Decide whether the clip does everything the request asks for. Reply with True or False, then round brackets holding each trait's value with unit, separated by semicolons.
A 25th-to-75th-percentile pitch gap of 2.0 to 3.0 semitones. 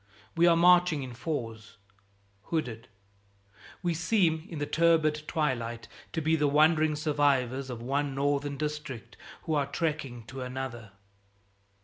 False (3.7 semitones)